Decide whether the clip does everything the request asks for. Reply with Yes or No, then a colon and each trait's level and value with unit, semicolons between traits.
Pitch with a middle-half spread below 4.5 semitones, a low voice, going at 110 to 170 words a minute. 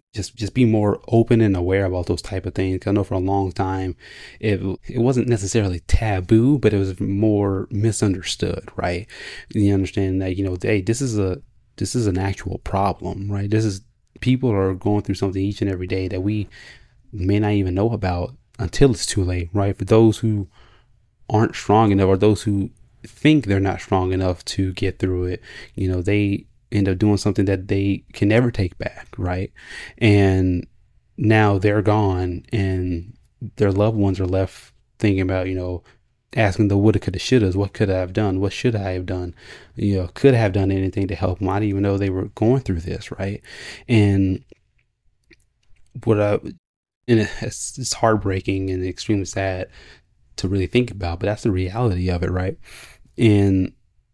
No: narrow, 2.6 semitones; low, 100 Hz; average, 190 wpm